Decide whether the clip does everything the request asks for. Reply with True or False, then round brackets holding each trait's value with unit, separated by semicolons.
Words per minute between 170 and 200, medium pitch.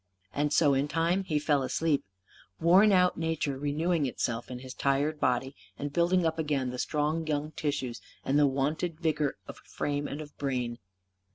True (175 wpm; 145 Hz)